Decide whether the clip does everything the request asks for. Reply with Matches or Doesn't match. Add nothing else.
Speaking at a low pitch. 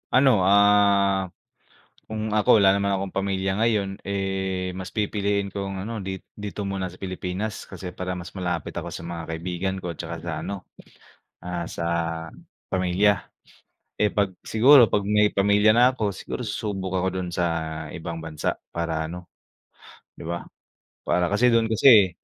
Matches